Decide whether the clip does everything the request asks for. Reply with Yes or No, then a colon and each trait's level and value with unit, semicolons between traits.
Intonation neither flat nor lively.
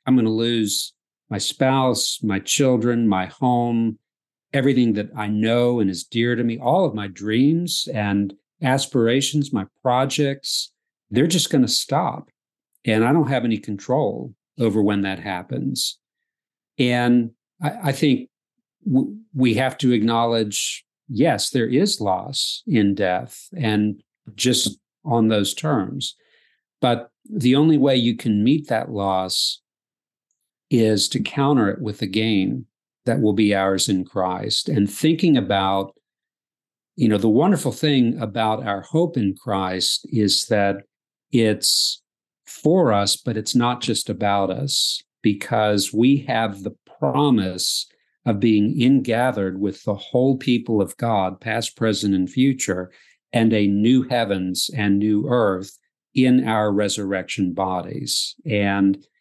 Yes: average, 4.1 semitones